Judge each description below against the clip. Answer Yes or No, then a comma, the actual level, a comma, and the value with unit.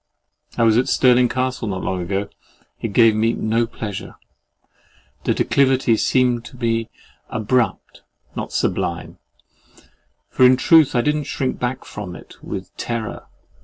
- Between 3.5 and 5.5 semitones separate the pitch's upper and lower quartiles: No, average, 2.7 semitones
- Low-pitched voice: Yes, low, 120 Hz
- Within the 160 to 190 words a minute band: No, average, 145 wpm